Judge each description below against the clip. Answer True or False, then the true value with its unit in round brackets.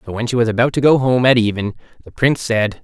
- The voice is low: True (115 Hz)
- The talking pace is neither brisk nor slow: False (275 wpm)